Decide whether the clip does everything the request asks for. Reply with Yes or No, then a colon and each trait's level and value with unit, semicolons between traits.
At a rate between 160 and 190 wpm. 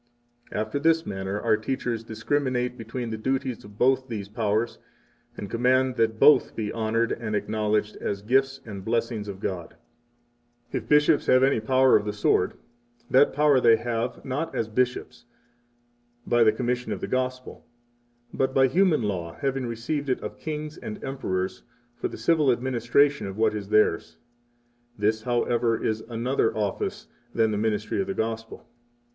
Yes: average, 165 wpm